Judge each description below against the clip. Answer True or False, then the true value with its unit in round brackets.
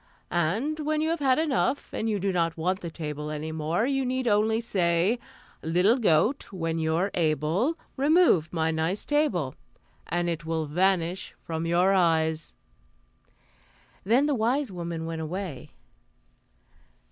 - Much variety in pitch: True (6.5 semitones)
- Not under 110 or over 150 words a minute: True (145 wpm)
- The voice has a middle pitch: True (180 Hz)